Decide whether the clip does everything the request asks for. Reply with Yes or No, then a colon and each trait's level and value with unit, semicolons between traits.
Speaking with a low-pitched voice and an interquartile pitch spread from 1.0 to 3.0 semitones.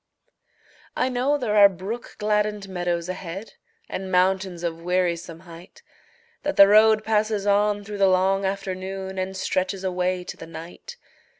No: high, 190 Hz; narrow, 2.4 semitones